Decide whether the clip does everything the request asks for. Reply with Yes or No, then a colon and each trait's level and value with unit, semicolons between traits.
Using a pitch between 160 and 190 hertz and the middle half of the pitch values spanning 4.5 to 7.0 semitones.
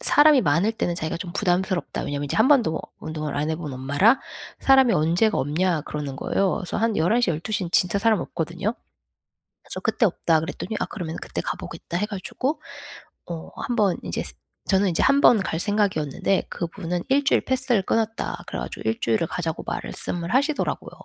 Yes: medium, 185 Hz; wide, 5.6 semitones